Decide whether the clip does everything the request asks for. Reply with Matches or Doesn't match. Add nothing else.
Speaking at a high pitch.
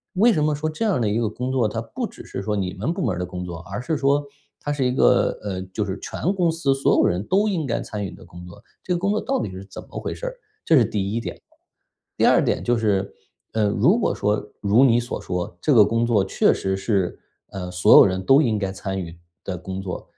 Doesn't match